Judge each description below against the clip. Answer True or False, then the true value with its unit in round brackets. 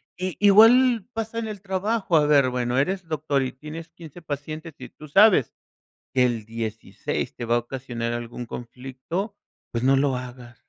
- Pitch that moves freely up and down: True (7.2 semitones)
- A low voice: False (145 Hz)